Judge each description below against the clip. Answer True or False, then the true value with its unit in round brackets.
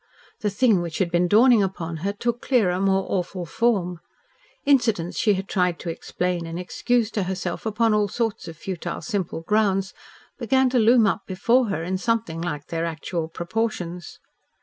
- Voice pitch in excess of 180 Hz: True (190 Hz)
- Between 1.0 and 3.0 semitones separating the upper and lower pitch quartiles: False (4.4 semitones)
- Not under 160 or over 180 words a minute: True (170 wpm)